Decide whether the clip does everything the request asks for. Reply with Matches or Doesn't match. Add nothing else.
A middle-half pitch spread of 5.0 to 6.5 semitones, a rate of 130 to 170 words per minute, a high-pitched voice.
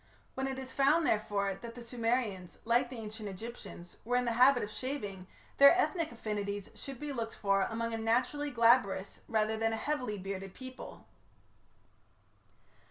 Doesn't match